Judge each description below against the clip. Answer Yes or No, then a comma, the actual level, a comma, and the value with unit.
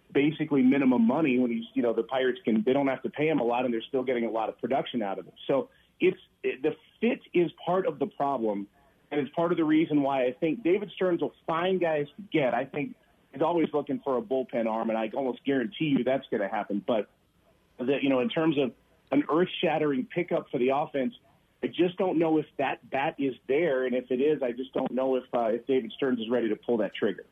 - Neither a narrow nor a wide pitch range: Yes, average, 4.5 semitones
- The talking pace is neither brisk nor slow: No, fast, 255 wpm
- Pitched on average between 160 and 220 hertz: No, medium, 140 Hz